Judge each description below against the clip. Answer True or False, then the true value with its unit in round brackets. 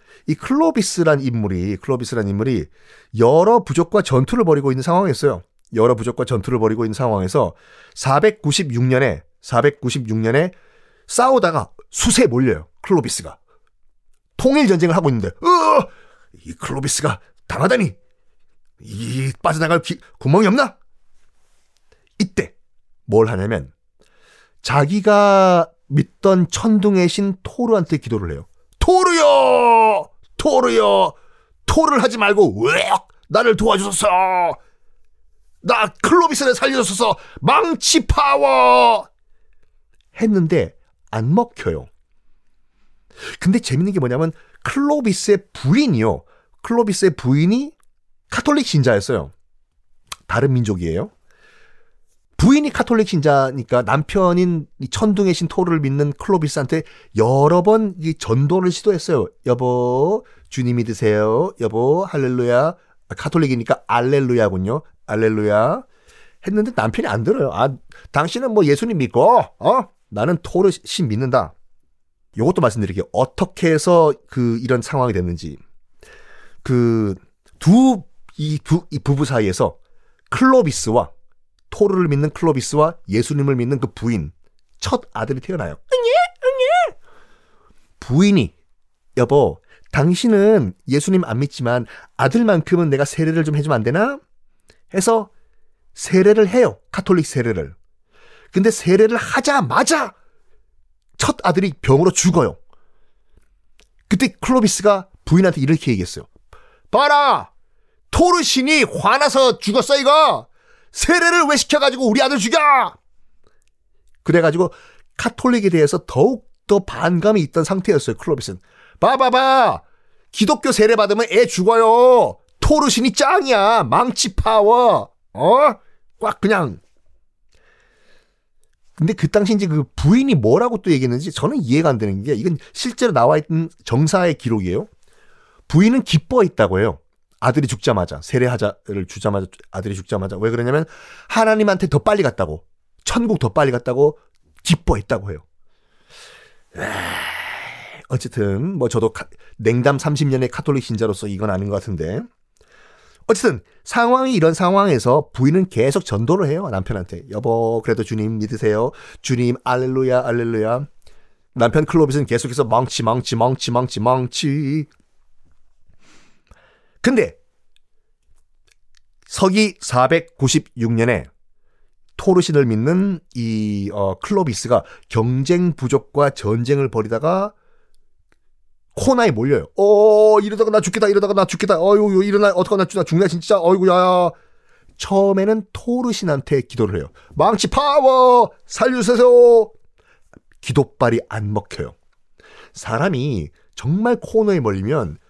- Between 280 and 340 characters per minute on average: False (270 characters per minute)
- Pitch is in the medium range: True (160 Hz)